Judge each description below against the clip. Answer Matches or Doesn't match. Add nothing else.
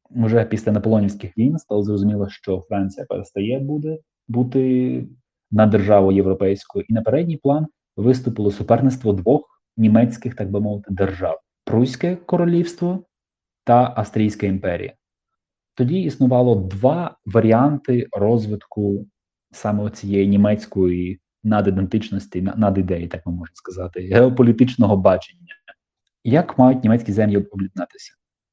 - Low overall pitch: Matches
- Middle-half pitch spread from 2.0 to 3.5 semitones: Doesn't match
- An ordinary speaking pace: Matches